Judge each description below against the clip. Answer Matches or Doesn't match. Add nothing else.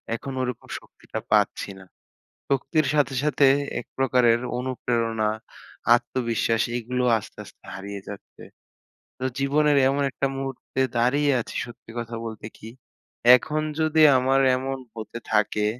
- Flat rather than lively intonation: Doesn't match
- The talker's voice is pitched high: Doesn't match